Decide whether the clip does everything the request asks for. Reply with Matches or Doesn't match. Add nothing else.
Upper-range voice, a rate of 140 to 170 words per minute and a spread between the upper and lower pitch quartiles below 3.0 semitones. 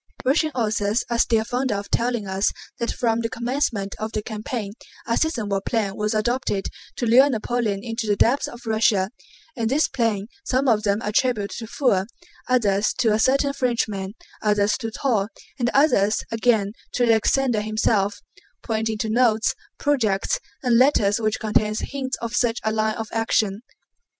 Matches